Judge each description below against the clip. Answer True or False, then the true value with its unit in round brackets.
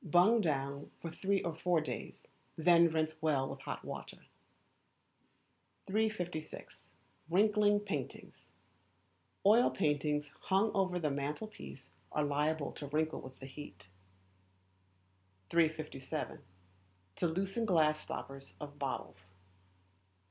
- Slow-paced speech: True (110 wpm)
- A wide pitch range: False (4.7 semitones)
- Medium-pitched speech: True (155 Hz)